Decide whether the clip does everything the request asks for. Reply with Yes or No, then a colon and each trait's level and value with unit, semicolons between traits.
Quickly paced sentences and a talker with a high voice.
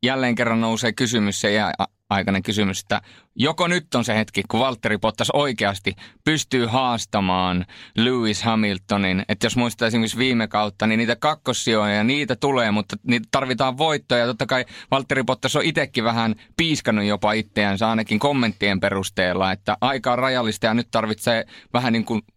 No: fast, 165 wpm; low, 115 Hz